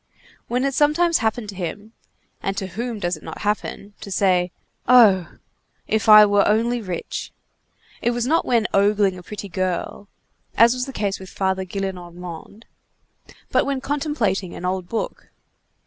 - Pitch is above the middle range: Yes, high, 205 Hz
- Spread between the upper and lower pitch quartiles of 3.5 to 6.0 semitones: Yes, average, 4.0 semitones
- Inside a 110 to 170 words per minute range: Yes, average, 150 wpm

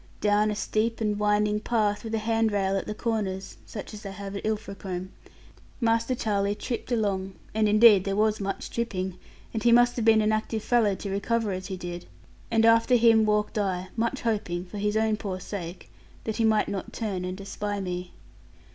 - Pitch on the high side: Yes, high, 210 Hz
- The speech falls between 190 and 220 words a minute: Yes, average, 195 wpm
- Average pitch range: No, narrow, 2.3 semitones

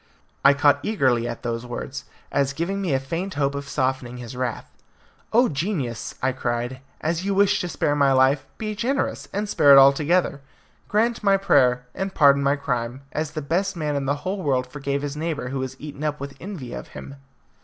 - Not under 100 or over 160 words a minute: No, average, 200 wpm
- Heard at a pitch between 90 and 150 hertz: Yes, medium, 140 Hz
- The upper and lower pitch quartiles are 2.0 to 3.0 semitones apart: No, average, 4.6 semitones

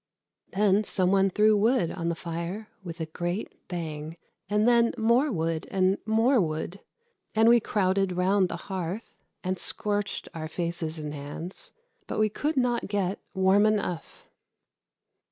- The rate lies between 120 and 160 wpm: Yes, average, 150 wpm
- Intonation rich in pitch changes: No, average, 4.0 semitones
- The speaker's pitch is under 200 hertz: Yes, high, 190 Hz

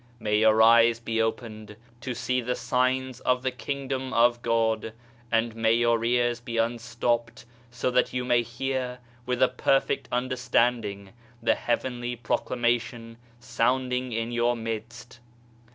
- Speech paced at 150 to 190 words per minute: No, slow, 135 wpm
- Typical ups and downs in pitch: No, narrow, 1.6 semitones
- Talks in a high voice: No, low, 120 Hz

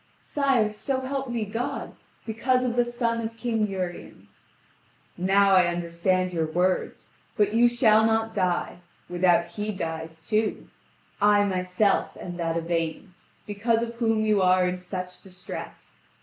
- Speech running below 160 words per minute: Yes, average, 145 wpm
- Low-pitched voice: No, high, 205 Hz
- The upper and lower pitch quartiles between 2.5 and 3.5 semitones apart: No, average, 3.9 semitones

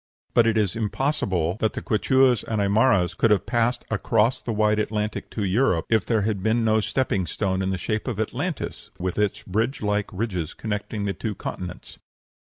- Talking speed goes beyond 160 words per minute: Yes, average, 195 wpm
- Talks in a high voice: No, low, 105 Hz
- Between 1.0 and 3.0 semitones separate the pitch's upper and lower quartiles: Yes, average, 2.7 semitones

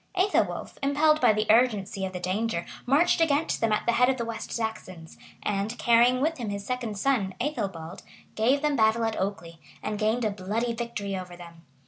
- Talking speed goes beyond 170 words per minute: Yes, average, 190 wpm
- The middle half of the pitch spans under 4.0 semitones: No, average, 4.3 semitones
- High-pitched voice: Yes, high, 220 Hz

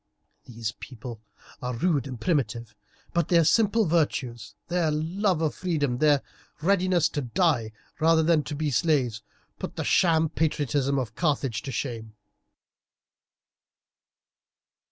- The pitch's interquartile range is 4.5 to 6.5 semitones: Yes, average, 5.3 semitones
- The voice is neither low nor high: Yes, medium, 150 Hz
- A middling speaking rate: No, slow, 125 wpm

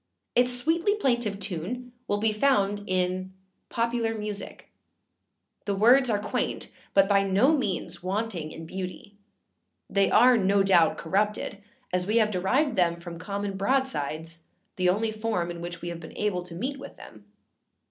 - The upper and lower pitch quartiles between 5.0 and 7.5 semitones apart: No, average, 4.2 semitones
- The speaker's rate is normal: Yes, average, 160 wpm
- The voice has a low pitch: No, high, 200 Hz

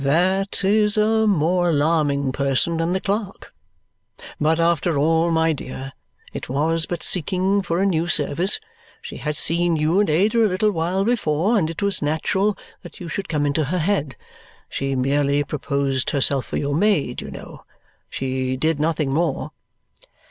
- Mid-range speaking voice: Yes, medium, 165 Hz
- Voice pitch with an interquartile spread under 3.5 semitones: No, average, 4.7 semitones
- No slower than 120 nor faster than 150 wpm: No, average, 165 wpm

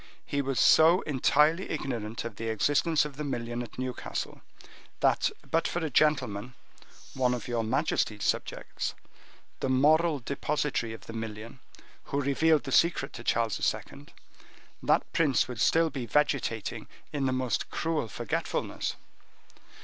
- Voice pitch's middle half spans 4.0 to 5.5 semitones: Yes, average, 4.4 semitones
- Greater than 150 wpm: No, average, 140 wpm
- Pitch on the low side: Yes, low, 130 Hz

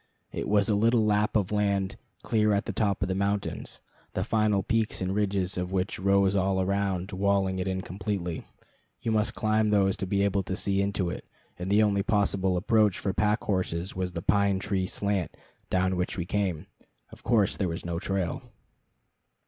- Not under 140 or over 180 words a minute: No, average, 190 wpm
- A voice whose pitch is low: Yes, low, 100 Hz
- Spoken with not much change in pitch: Yes, narrow, 1.9 semitones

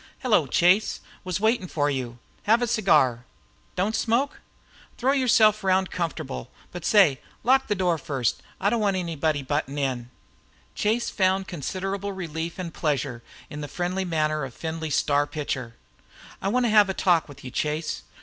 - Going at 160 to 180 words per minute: Yes, average, 170 wpm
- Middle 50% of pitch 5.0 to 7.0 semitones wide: Yes, wide, 5.6 semitones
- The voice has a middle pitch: Yes, medium, 175 Hz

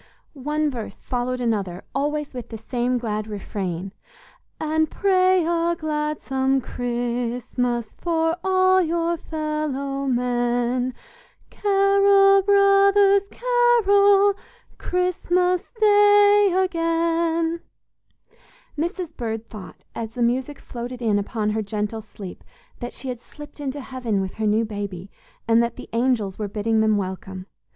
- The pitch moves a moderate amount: No, wide, 7.3 semitones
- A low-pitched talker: No, very high, 265 Hz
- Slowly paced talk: Yes, slow, 120 wpm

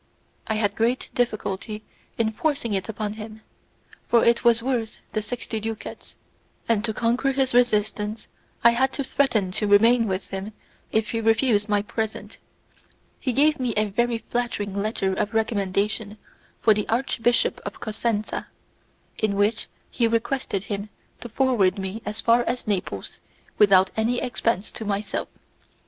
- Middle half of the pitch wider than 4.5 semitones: No, narrow, 2.4 semitones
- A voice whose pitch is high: Yes, high, 220 Hz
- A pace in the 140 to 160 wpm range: Yes, average, 150 wpm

